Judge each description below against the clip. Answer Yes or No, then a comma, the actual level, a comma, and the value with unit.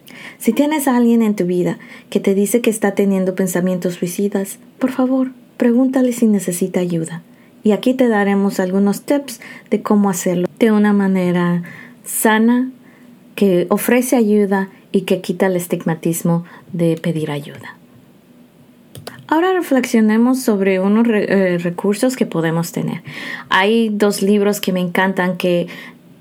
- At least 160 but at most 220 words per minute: No, average, 140 wpm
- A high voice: Yes, high, 205 Hz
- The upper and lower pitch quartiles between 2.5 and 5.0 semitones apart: Yes, average, 4.5 semitones